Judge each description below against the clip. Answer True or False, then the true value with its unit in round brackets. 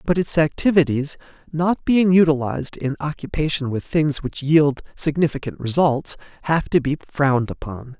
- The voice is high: False (150 Hz)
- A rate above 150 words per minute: False (145 wpm)